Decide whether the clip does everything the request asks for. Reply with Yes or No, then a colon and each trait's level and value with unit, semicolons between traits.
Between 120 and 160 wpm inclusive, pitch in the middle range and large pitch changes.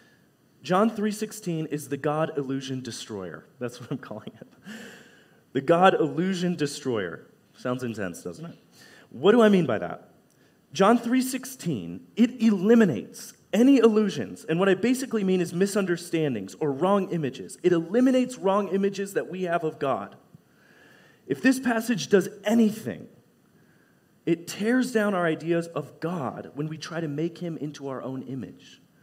Yes: average, 150 wpm; medium, 175 Hz; wide, 6.6 semitones